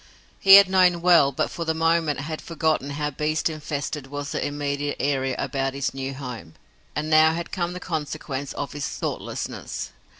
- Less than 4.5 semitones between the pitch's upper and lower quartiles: Yes, average, 2.7 semitones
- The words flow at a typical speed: Yes, average, 175 wpm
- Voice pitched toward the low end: No, medium, 150 Hz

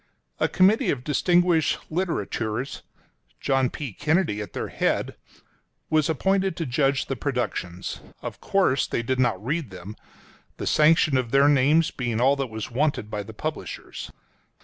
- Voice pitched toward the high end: No, low, 135 Hz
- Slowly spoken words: No, average, 165 wpm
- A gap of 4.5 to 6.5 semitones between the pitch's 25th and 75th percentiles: Yes, average, 5.2 semitones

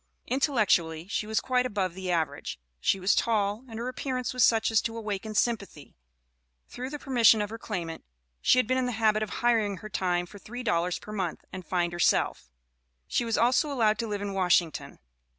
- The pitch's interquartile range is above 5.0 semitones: No, average, 4.3 semitones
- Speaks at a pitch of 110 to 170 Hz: No, high, 215 Hz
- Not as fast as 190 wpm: No, average, 200 wpm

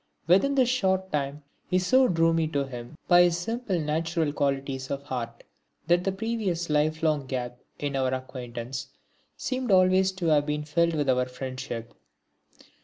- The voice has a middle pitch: Yes, medium, 155 Hz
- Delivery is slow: No, average, 165 wpm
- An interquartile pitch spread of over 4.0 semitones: Yes, wide, 5.4 semitones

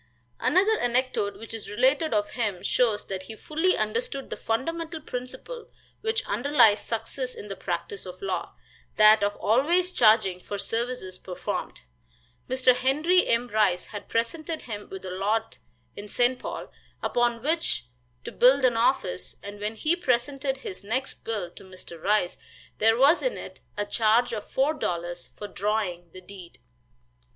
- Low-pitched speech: No, high, 230 Hz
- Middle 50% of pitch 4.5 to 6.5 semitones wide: Yes, average, 4.8 semitones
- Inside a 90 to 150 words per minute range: No, average, 160 wpm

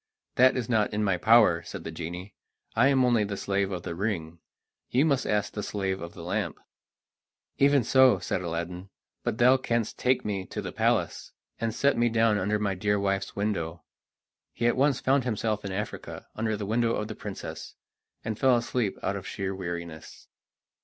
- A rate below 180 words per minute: No, average, 190 wpm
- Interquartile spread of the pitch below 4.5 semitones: Yes, average, 3.9 semitones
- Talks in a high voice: No, low, 105 Hz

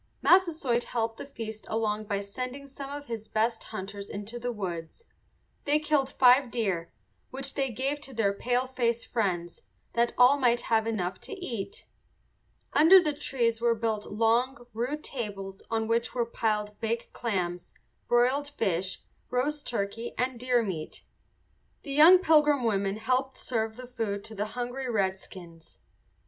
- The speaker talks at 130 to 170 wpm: Yes, average, 150 wpm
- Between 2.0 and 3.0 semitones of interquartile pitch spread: No, average, 3.9 semitones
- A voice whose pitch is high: Yes, high, 235 Hz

